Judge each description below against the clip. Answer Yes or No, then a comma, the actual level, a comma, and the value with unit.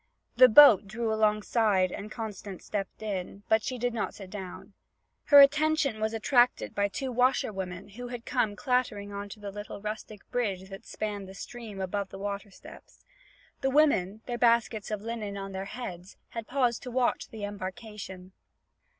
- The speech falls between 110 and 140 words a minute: No, average, 175 wpm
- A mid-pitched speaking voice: No, high, 215 Hz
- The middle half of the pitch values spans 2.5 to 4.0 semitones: Yes, average, 3.4 semitones